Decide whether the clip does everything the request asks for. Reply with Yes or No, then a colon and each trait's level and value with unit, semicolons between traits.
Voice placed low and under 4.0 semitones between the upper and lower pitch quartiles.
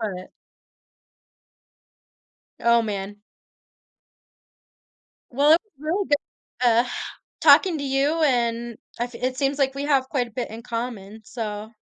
No: high, 245 Hz; average, 3.6 semitones